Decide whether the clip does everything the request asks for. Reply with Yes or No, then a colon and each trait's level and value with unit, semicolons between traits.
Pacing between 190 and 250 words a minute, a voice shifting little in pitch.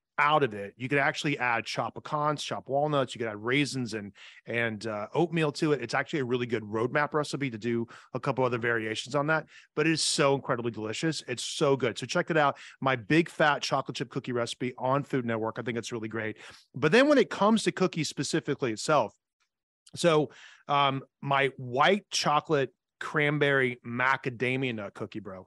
No: average, 195 wpm; average, 4.1 semitones